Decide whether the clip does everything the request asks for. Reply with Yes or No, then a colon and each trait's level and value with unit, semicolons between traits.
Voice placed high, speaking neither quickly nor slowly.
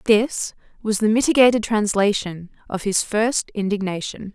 No: high, 210 Hz; slow, 125 wpm